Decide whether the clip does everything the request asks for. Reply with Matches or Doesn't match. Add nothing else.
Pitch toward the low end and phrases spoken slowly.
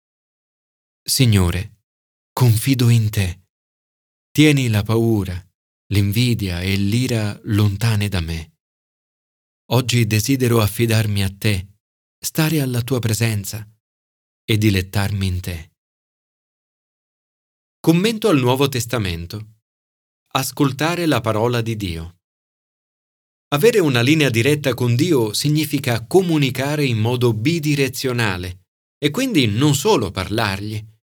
Matches